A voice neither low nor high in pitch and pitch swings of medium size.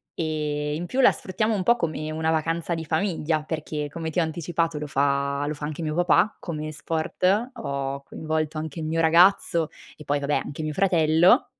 No: medium, 160 Hz; narrow, 2.1 semitones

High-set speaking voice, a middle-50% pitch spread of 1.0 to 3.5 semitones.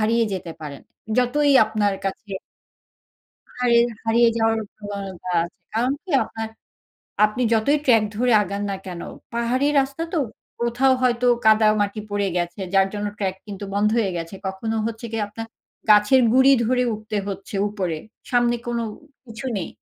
Yes: high, 220 Hz; average, 3.1 semitones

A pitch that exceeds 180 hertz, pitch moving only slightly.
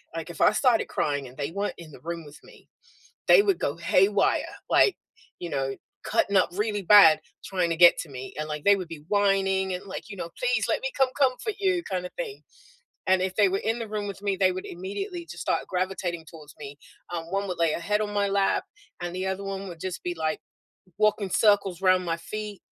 No: high, 190 Hz; average, 3.5 semitones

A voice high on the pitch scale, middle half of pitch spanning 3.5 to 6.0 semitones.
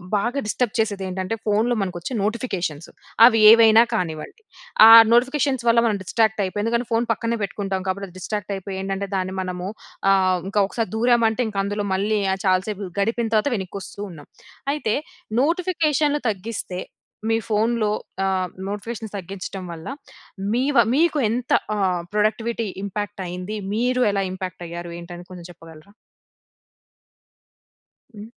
Yes: high, 205 Hz; average, 3.8 semitones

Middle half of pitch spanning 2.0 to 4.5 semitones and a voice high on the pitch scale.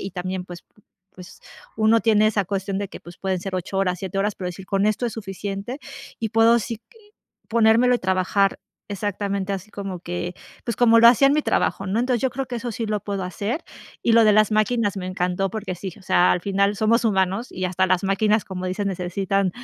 Yes: average, 2.9 semitones; high, 200 Hz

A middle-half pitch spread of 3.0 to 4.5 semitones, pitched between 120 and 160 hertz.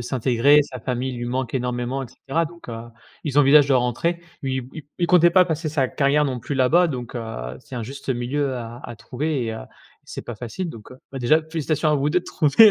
Yes: average, 3.9 semitones; low, 135 Hz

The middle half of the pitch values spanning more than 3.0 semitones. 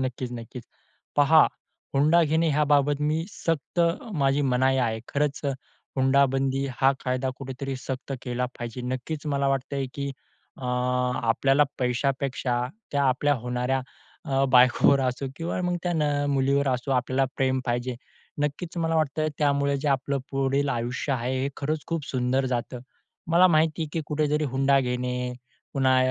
No: narrow, 2.4 semitones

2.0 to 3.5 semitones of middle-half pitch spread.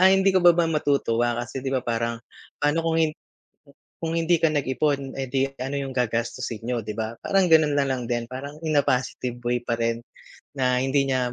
No: average, 3.9 semitones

